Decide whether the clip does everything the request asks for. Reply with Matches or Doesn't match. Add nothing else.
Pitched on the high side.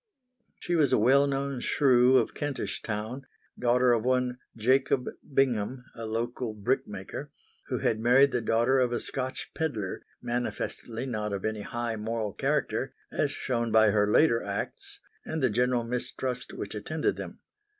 Doesn't match